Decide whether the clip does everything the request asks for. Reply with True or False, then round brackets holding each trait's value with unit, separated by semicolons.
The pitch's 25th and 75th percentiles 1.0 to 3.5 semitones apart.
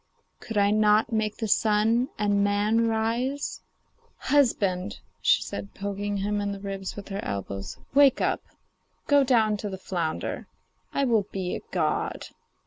True (2.4 semitones)